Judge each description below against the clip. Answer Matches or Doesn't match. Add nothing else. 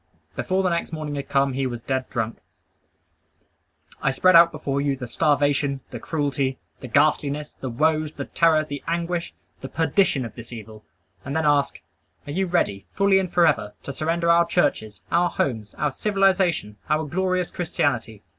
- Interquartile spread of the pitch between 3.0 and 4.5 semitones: Matches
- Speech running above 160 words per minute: Matches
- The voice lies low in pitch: Doesn't match